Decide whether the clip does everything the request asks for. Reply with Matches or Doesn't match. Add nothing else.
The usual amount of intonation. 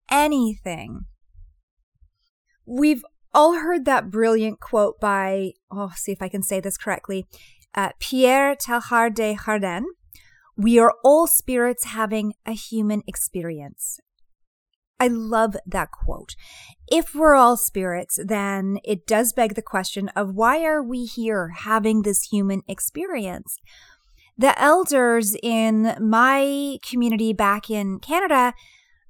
Matches